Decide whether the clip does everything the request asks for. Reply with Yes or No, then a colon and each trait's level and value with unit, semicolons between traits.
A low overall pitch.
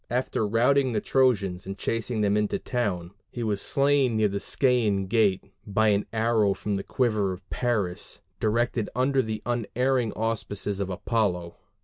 Yes: low, 110 Hz